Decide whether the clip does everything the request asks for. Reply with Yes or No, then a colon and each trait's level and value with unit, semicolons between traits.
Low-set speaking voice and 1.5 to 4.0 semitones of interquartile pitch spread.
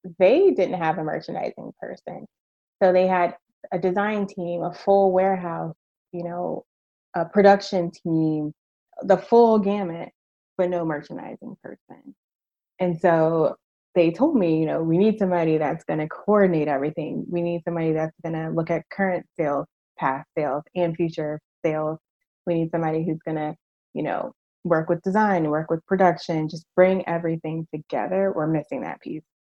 No: medium, 175 Hz; average, 3.1 semitones